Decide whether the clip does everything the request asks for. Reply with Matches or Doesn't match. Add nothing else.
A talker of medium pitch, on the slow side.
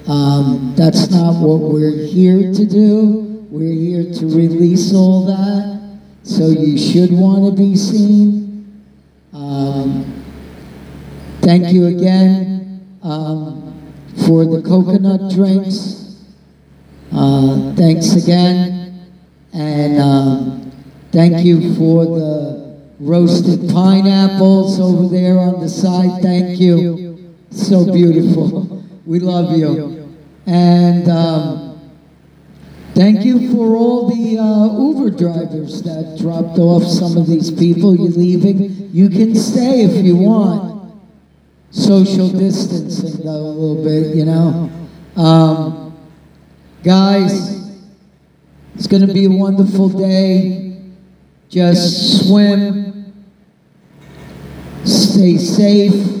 Matches